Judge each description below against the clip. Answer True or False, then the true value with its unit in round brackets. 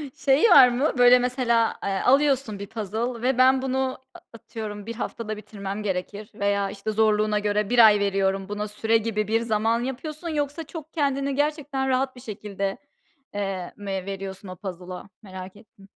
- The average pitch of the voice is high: True (220 Hz)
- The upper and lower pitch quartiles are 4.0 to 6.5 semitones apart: True (4.4 semitones)